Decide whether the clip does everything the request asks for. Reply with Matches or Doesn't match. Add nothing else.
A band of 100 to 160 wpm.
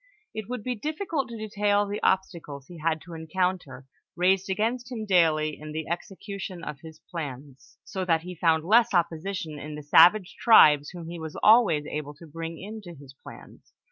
Doesn't match